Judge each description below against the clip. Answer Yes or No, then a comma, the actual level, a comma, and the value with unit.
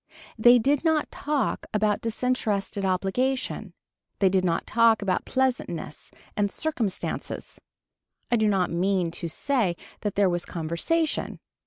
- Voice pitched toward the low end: No, high, 210 Hz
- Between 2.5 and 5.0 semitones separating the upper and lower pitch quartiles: No, wide, 5.4 semitones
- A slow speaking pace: Yes, slow, 130 wpm